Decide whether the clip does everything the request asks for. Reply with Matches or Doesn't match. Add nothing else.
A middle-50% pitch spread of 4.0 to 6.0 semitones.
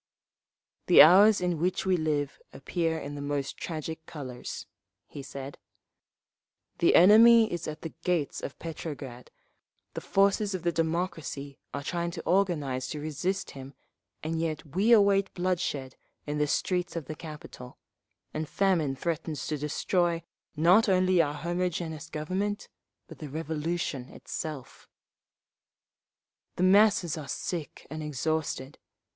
Doesn't match